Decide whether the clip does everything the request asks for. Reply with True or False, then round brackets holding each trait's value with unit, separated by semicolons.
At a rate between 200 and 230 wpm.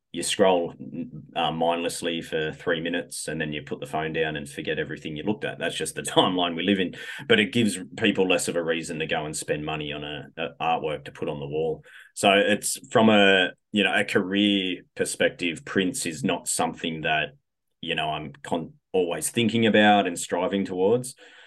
True (205 wpm)